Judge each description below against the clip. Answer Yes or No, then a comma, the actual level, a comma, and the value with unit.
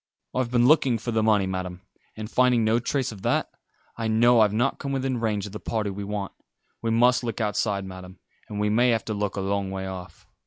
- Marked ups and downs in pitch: No, average, 3.2 semitones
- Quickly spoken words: Yes, fast, 230 wpm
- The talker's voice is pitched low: Yes, low, 110 Hz